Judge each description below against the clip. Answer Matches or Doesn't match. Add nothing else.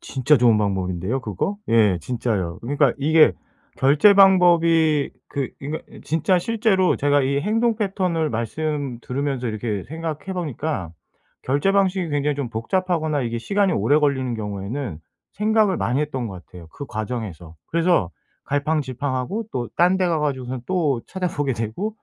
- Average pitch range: Doesn't match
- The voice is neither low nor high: Matches